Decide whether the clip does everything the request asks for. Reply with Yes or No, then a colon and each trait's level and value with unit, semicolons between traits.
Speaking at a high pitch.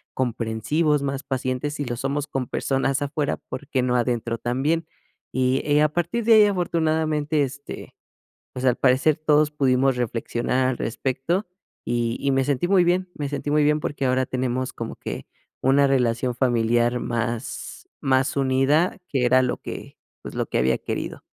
No: low, 135 Hz